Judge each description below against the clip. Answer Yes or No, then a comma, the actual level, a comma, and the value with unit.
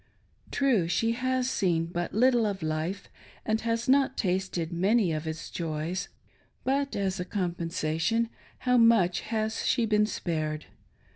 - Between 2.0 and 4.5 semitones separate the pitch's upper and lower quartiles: No, wide, 5.4 semitones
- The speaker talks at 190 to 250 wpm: No, average, 140 wpm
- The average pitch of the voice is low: No, high, 195 Hz